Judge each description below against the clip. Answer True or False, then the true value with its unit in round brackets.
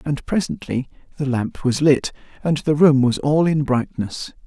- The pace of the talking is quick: False (175 wpm)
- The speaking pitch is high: False (140 Hz)